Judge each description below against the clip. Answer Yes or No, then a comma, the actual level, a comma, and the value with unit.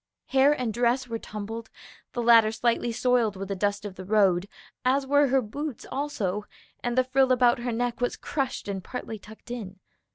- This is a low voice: No, high, 235 Hz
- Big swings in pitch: No, average, 3.5 semitones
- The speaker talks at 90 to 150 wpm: No, average, 190 wpm